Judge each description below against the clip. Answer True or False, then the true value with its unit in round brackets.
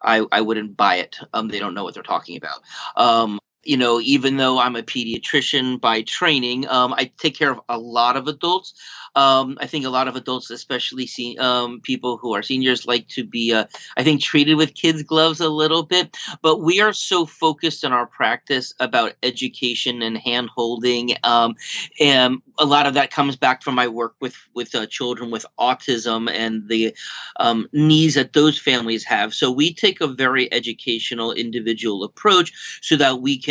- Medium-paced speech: True (195 wpm)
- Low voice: True (125 Hz)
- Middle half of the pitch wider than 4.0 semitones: False (3.6 semitones)